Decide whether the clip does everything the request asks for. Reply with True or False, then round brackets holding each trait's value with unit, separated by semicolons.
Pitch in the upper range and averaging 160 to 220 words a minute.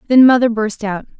True (230 Hz; 200 wpm)